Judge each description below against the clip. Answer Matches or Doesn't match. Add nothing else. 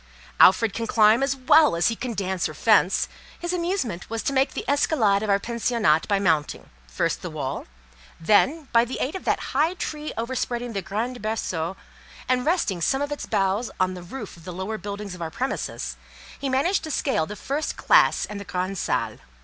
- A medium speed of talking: Matches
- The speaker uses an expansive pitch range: Matches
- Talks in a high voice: Matches